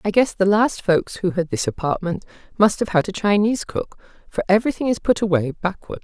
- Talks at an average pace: No, fast, 210 wpm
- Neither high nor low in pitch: No, high, 195 Hz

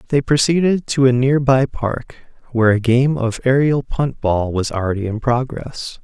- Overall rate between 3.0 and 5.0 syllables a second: Yes, 4.6 syllables/s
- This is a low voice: Yes, low, 125 Hz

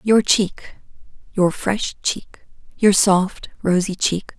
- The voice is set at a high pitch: Yes, high, 195 Hz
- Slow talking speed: Yes, slow, 110 wpm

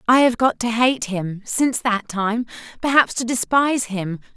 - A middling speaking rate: Yes, average, 165 wpm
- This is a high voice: Yes, high, 230 Hz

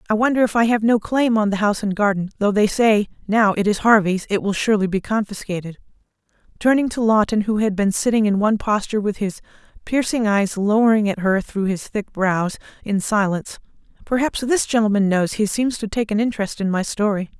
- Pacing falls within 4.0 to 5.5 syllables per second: No, 5.8 syllables/s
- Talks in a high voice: Yes, high, 210 Hz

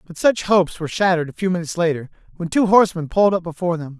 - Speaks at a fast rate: Yes, fast, 240 wpm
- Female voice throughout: No, male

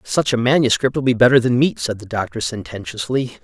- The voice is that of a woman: No, male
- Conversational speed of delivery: Yes, average, 190 wpm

